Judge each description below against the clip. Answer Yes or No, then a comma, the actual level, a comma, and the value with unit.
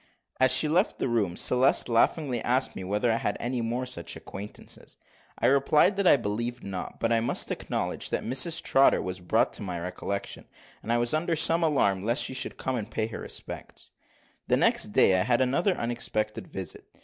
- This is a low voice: Yes, low, 120 Hz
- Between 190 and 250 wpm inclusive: Yes, fast, 205 wpm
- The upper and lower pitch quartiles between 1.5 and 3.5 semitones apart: No, average, 4.3 semitones